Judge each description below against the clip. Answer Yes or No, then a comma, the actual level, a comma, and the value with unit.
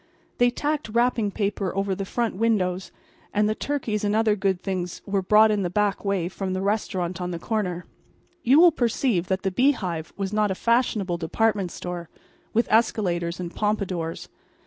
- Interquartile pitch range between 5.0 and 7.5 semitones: No, average, 3.4 semitones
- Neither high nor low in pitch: No, high, 200 Hz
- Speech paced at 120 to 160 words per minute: No, average, 180 wpm